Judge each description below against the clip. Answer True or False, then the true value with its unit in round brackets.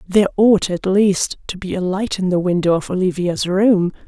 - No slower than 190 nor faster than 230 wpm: True (205 wpm)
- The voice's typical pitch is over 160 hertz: True (190 Hz)